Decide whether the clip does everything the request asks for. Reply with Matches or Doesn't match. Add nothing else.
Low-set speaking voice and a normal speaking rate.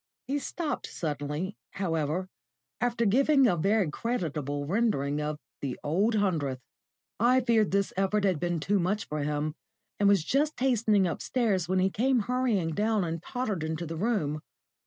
Doesn't match